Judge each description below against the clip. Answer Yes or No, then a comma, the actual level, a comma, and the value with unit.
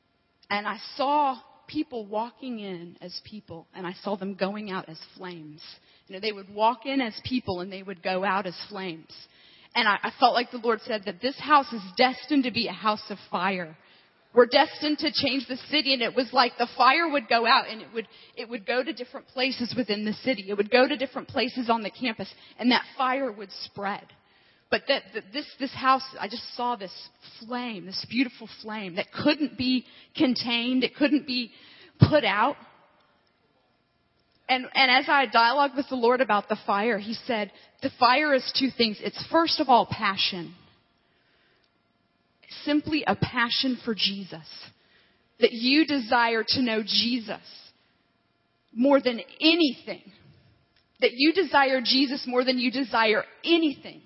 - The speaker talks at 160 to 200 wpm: Yes, average, 180 wpm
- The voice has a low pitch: No, high, 245 Hz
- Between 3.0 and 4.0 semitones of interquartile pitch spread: No, average, 4.4 semitones